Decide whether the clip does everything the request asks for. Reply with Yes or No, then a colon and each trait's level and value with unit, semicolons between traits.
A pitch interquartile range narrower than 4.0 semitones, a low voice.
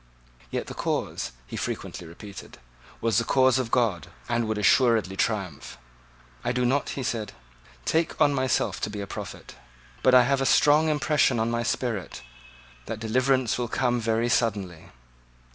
Yes: average, 3.5 semitones; low, 115 Hz